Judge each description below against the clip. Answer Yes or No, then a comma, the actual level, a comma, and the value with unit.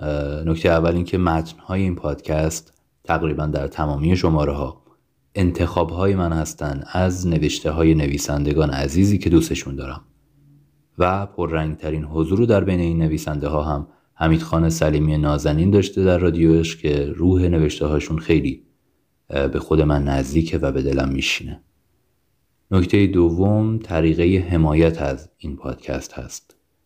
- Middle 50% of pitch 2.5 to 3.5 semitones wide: Yes, average, 3.0 semitones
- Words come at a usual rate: Yes, average, 140 wpm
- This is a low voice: Yes, very low, 80 Hz